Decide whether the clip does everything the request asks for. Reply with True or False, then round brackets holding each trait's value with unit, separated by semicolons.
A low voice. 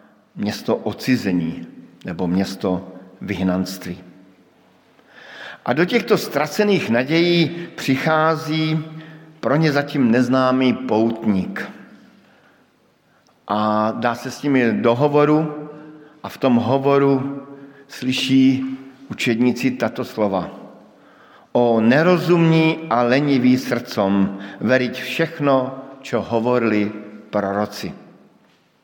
True (130 Hz)